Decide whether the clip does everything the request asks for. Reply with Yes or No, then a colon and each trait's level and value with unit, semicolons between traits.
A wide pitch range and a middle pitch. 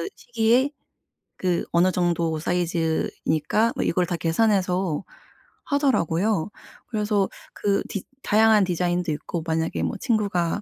No: average, 4.1 semitones; medium, 180 Hz